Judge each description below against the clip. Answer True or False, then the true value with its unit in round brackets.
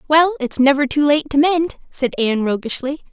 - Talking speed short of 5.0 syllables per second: False (5.1 syllables/s)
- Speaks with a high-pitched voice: True (280 Hz)